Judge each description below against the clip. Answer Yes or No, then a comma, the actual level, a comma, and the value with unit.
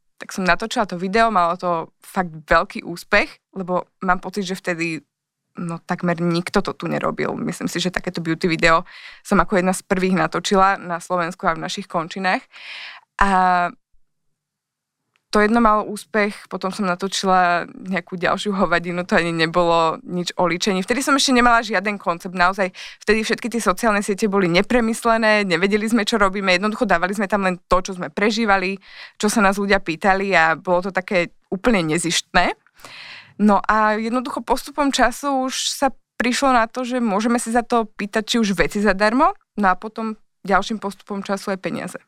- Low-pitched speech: No, high, 195 Hz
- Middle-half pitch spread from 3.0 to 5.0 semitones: Yes, average, 3.7 semitones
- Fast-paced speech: Yes, fast, 175 wpm